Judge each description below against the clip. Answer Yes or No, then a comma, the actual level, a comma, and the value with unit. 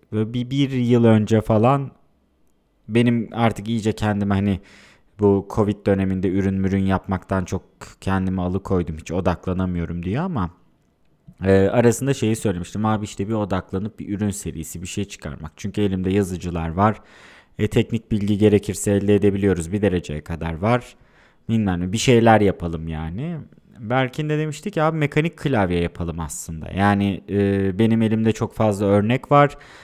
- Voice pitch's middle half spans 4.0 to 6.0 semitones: No, average, 3.3 semitones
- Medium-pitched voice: No, low, 100 Hz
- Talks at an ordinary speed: No, fast, 150 wpm